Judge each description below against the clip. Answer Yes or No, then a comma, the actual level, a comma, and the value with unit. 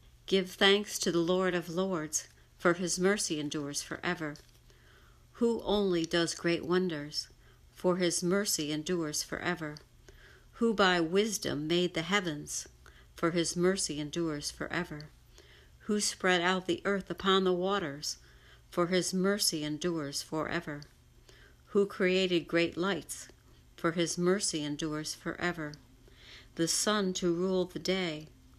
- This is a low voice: No, medium, 170 Hz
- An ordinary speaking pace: No, slow, 130 wpm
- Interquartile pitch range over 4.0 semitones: No, average, 3.4 semitones